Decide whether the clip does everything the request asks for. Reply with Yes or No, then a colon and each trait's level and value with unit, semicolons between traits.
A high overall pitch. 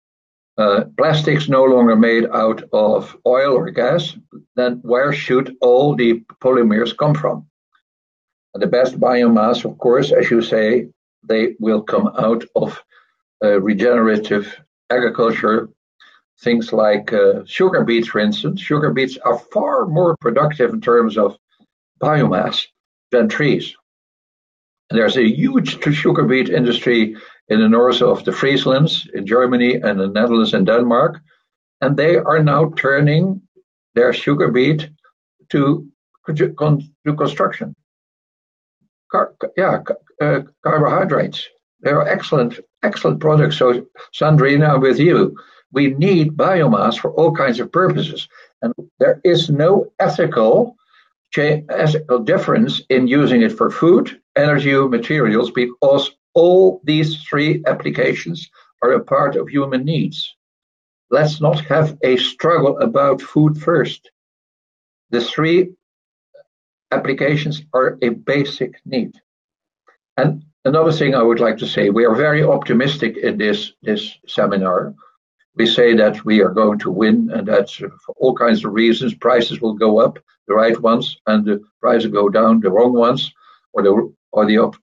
No: low, 135 Hz